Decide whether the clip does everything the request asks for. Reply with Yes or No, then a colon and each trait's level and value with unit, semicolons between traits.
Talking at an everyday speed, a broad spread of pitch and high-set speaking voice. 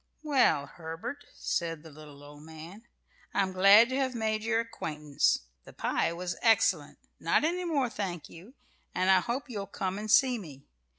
Yes: average, 170 wpm; wide, 6.5 semitones; high, 195 Hz